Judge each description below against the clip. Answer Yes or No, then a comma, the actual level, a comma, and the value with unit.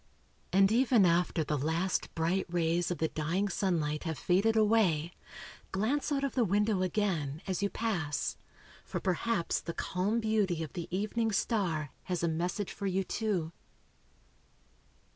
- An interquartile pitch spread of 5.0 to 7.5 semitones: No, average, 4.3 semitones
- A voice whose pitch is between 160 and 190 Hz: Yes, medium, 185 Hz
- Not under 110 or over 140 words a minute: No, average, 150 wpm